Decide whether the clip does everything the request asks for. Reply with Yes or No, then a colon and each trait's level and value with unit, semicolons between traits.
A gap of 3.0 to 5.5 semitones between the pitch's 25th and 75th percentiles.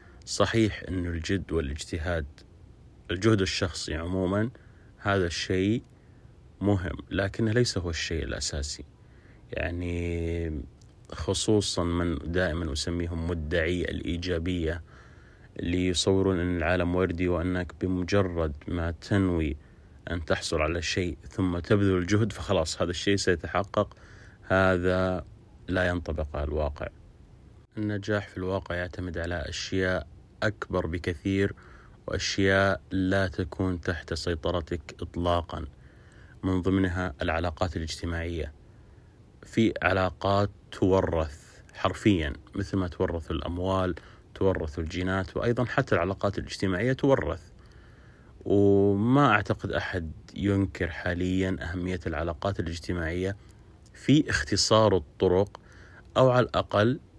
No: narrow, 2.5 semitones